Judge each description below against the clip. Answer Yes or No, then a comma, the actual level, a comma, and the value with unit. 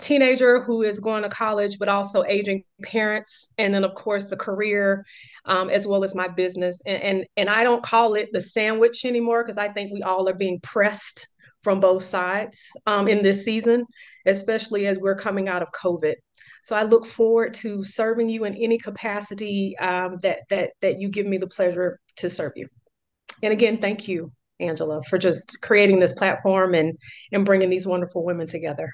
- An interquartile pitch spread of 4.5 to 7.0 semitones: No, narrow, 2.6 semitones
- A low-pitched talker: No, high, 200 Hz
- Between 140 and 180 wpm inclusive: No, average, 195 wpm